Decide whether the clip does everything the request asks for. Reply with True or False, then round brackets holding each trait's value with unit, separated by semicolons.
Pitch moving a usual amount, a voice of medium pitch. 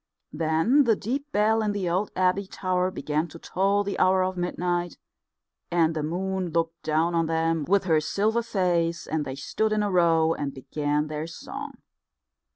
True (3.4 semitones; 175 Hz)